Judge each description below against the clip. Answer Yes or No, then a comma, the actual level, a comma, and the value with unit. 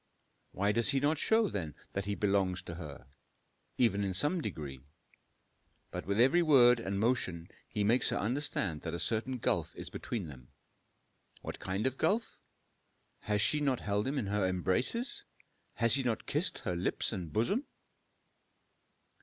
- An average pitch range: No, wide, 6.1 semitones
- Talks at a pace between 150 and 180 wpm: Yes, average, 160 wpm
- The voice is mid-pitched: No, low, 105 Hz